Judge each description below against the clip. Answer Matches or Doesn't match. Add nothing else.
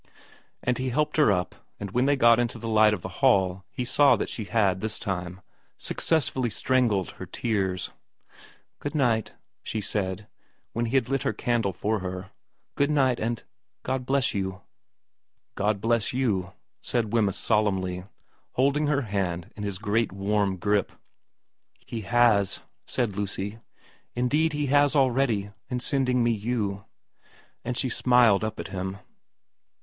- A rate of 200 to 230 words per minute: Doesn't match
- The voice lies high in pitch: Doesn't match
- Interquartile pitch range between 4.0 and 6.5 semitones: Matches